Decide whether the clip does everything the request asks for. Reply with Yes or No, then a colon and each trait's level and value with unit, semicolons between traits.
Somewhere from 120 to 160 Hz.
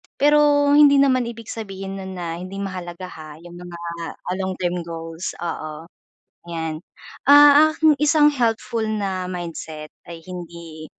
No: medium, 185 Hz